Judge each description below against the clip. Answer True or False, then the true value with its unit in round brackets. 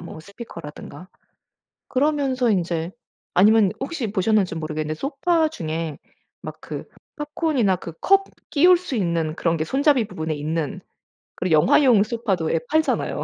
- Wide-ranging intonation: True (9.0 semitones)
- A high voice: True (200 Hz)